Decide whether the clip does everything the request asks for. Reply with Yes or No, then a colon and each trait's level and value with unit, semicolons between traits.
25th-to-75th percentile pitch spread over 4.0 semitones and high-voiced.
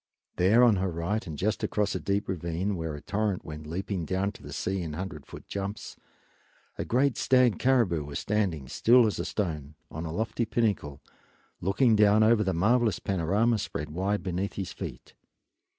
No: average, 4.5 semitones; very low, 95 Hz